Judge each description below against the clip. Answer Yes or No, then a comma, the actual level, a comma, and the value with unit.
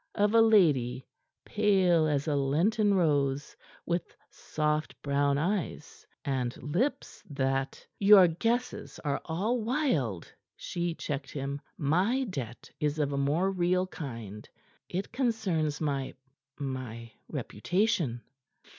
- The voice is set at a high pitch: No, medium, 155 Hz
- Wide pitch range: Yes, wide, 6.1 semitones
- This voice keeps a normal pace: No, slow, 120 wpm